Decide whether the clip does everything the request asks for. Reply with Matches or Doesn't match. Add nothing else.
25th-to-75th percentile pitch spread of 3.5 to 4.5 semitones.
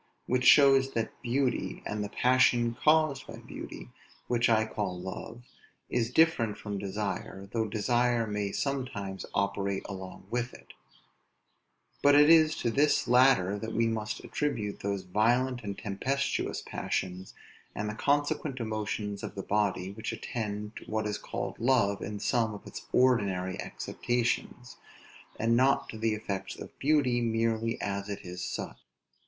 Matches